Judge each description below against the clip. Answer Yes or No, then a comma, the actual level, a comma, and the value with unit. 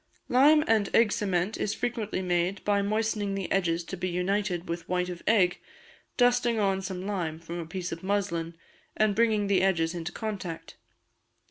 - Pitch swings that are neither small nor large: Yes, average, 3.2 semitones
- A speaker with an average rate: Yes, average, 170 wpm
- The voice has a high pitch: Yes, high, 195 Hz